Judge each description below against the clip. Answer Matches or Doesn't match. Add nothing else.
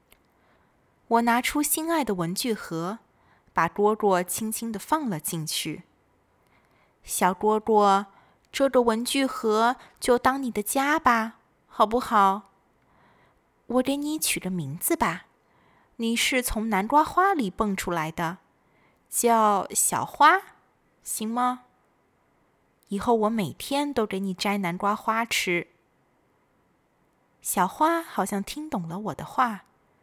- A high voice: Matches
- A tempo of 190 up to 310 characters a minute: Doesn't match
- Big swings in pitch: Doesn't match